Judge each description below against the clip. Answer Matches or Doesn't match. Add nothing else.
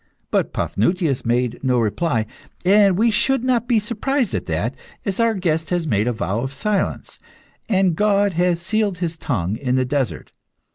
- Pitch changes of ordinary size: Doesn't match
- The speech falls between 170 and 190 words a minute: Matches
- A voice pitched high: Doesn't match